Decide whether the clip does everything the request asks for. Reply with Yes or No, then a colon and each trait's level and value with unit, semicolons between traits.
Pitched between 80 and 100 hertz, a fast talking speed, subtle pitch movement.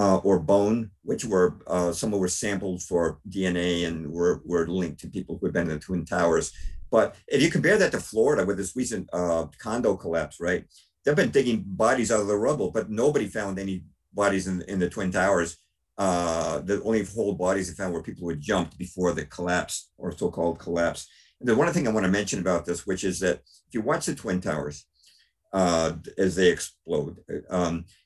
Yes: very low, 90 Hz; fast, 215 wpm; narrow, 2.3 semitones